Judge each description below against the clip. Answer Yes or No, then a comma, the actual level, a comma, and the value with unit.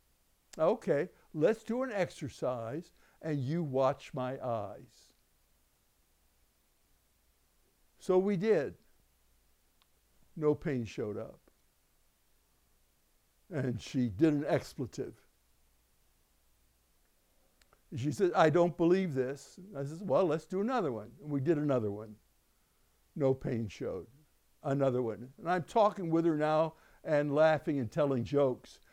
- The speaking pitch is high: No, low, 135 Hz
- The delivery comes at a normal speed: No, slow, 120 wpm